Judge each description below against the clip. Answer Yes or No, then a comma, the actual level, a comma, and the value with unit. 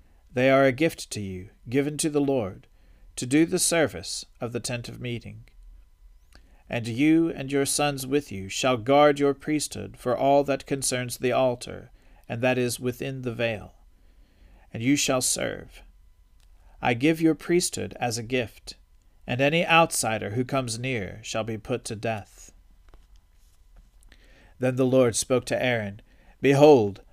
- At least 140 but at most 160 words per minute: Yes, average, 155 wpm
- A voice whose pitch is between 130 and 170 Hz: No, low, 120 Hz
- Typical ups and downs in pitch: No, wide, 6.7 semitones